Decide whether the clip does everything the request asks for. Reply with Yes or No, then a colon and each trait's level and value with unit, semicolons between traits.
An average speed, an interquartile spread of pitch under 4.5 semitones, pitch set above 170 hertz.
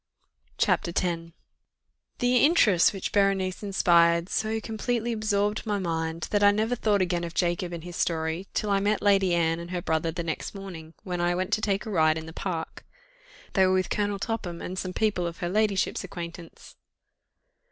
Yes: average, 185 wpm; average, 3.4 semitones; medium, 185 Hz